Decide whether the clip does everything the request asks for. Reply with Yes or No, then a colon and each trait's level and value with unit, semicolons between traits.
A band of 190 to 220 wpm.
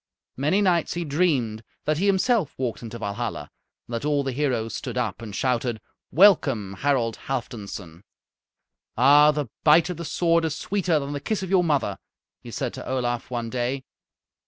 No: average, 175 wpm